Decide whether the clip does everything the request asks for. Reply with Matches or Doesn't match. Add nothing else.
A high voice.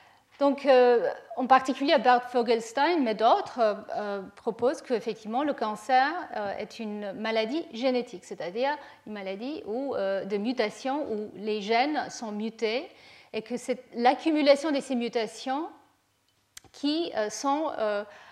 Matches